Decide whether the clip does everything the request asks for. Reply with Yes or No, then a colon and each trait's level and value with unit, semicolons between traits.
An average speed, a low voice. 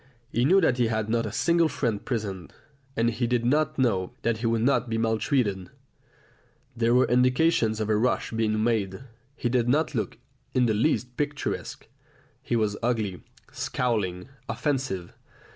Yes: average, 160 wpm; low, 115 Hz